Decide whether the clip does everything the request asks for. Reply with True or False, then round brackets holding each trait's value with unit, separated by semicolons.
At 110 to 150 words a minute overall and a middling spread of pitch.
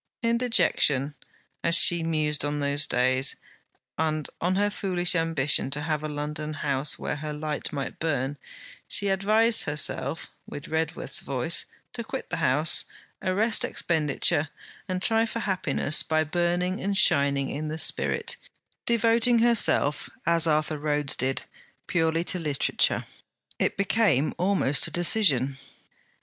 True (135 wpm; 4.3 semitones)